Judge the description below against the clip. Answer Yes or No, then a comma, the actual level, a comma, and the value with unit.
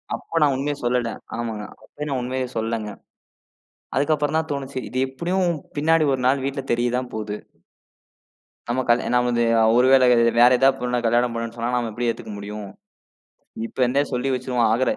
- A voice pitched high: No, low, 125 Hz